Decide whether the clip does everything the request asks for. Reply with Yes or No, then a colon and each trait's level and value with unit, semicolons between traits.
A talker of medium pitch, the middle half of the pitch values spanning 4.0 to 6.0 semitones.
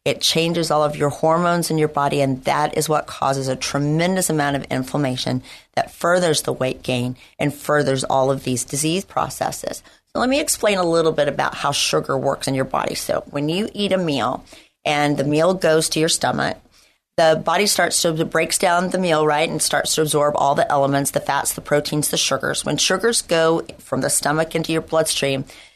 No: medium, 155 Hz; average, 2.8 semitones